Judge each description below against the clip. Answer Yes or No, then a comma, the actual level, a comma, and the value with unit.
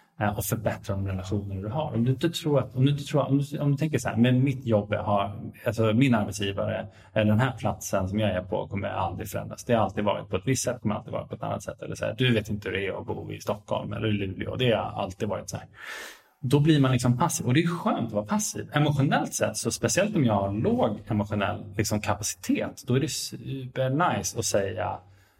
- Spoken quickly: Yes, fast, 220 wpm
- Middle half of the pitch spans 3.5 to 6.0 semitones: Yes, average, 4.0 semitones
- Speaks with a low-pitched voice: Yes, low, 115 Hz